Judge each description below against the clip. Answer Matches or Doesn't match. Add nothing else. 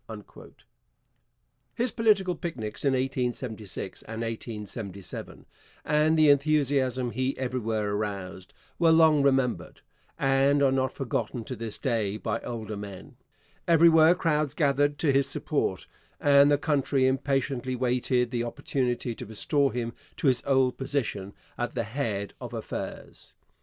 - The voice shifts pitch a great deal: Doesn't match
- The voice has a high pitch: Doesn't match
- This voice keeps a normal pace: Doesn't match